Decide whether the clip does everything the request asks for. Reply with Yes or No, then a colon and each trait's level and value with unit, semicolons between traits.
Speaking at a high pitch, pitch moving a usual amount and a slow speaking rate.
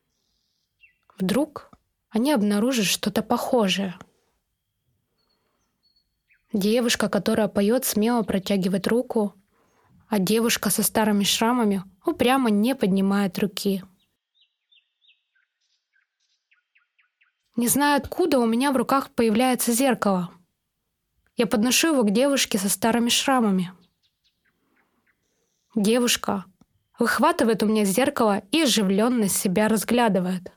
Yes: high, 225 Hz; average, 3.4 semitones; slow, 90 wpm